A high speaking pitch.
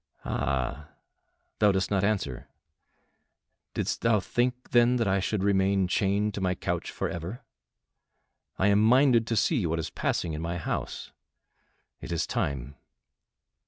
No: very low, 95 Hz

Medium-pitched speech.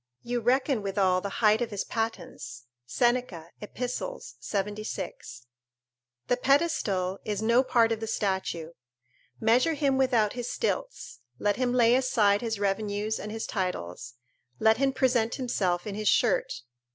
No: high, 220 Hz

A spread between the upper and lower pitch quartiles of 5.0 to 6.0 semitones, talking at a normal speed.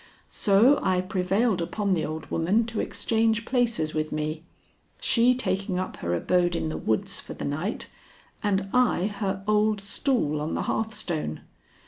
Yes: average, 5.3 semitones; average, 155 wpm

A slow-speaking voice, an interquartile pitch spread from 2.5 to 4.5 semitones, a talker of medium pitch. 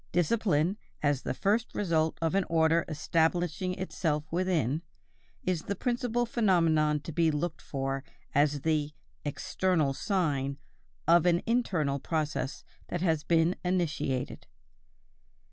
Yes: slow, 120 wpm; average, 3.6 semitones; medium, 165 Hz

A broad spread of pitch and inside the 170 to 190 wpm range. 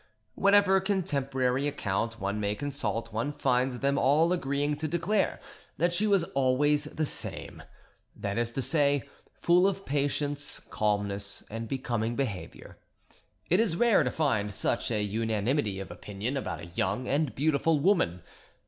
No: wide, 5.9 semitones; average, 145 wpm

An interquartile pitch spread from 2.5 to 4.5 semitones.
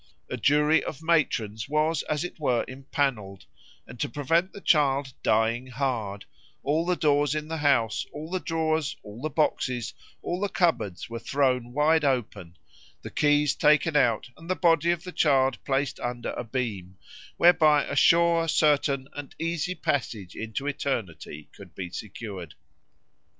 No: average, 4.9 semitones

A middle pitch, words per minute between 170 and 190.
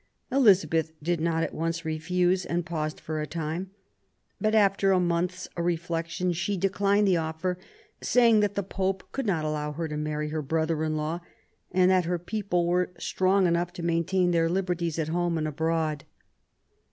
Yes: medium, 170 Hz; average, 175 wpm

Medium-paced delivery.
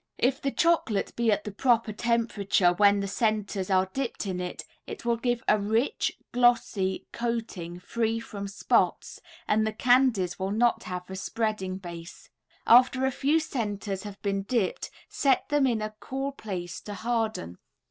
Yes: average, 165 wpm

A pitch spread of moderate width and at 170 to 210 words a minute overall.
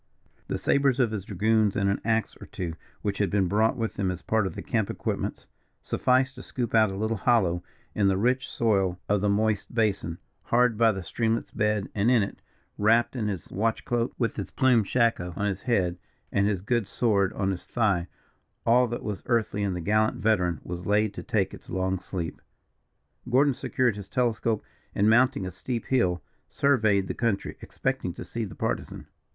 Yes: average, 3.3 semitones; average, 195 wpm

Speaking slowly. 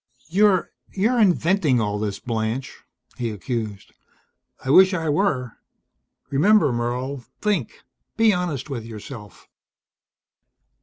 Yes: slow, 105 wpm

